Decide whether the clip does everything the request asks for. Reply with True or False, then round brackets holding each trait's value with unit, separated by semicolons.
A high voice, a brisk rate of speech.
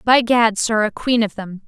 True (220 Hz; 250 wpm)